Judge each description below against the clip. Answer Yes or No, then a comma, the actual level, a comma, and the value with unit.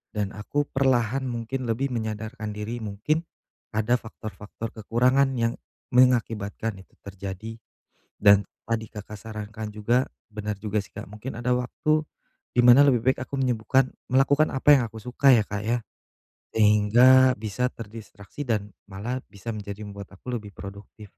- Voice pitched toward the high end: No, low, 115 Hz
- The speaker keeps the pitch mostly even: No, average, 3.2 semitones